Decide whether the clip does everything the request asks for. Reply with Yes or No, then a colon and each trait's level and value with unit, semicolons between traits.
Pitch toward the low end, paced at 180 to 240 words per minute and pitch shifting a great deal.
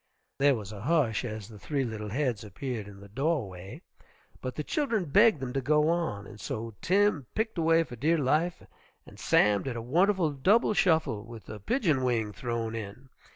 Yes: low, 130 Hz; average, 190 wpm; wide, 7.0 semitones